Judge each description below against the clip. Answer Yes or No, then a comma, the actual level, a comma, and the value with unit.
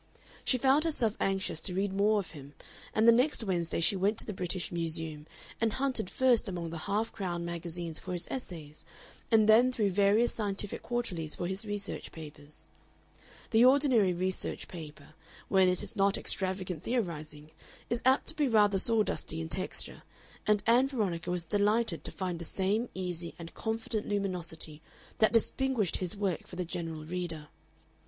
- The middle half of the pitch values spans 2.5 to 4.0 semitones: No, average, 4.6 semitones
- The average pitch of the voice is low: No, high, 190 Hz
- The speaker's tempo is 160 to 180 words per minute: Yes, average, 170 wpm